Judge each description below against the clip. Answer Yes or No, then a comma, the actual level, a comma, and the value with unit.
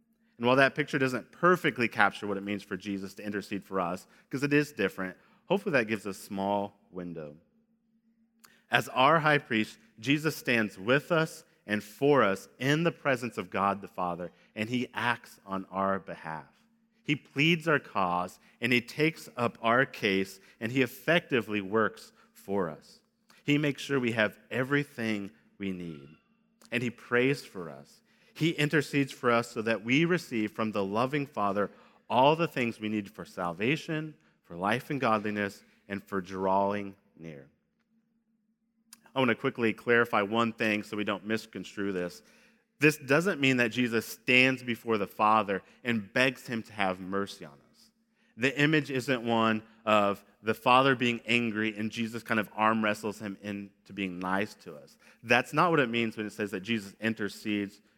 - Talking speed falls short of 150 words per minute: No, average, 175 wpm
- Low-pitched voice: Yes, low, 115 Hz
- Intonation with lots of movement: Yes, wide, 6.1 semitones